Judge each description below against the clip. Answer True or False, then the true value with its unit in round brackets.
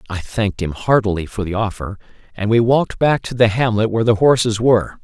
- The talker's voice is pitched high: False (110 Hz)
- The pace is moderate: False (215 wpm)